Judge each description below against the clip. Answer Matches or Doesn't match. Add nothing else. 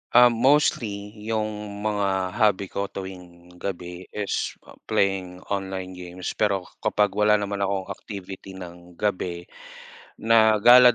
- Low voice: Matches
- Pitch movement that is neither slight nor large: Doesn't match